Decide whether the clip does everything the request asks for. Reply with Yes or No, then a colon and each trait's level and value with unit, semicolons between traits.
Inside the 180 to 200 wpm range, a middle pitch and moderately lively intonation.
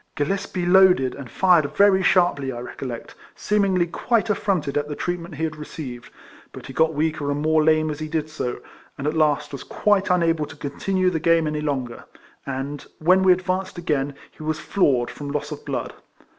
Yes: average, 190 wpm; medium, 155 Hz; average, 4.0 semitones